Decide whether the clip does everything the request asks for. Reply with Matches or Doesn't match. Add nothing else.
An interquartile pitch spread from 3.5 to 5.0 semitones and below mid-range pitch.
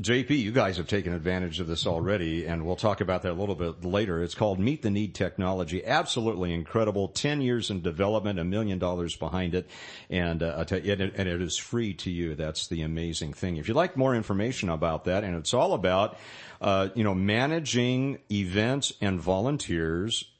Matches